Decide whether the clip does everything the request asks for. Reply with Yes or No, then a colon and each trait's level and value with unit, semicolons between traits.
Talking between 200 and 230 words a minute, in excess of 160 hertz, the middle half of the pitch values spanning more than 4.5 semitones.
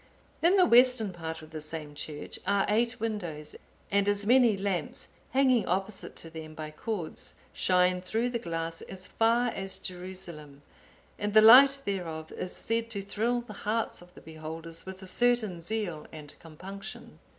No: average, 165 wpm; high, 190 Hz; wide, 5.6 semitones